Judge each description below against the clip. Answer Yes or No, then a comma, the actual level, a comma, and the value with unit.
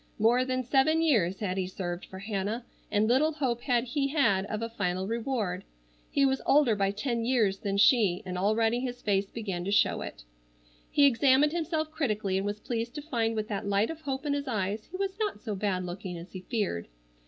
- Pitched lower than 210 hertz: No, high, 225 Hz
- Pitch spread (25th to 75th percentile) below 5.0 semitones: No, average, 5.3 semitones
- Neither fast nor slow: No, fast, 210 wpm